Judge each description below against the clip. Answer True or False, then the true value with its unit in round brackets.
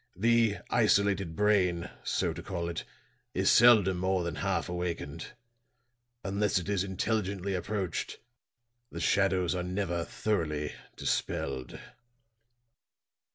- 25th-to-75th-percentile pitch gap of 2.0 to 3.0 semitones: True (2.7 semitones)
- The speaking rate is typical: False (110 wpm)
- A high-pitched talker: False (95 Hz)